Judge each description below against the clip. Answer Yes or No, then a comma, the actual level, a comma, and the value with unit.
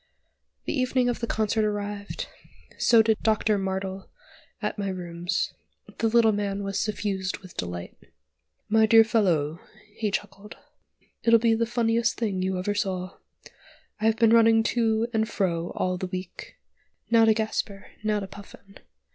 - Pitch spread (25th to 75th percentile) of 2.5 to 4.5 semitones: Yes, average, 2.8 semitones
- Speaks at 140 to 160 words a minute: Yes, average, 150 wpm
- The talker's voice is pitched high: Yes, high, 210 Hz